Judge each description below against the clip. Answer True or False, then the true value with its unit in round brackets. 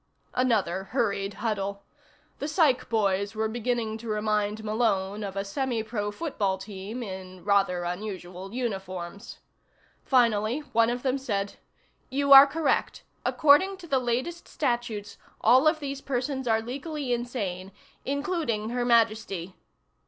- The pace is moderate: False (130 wpm)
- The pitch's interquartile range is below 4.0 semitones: False (4.5 semitones)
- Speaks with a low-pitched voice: False (225 Hz)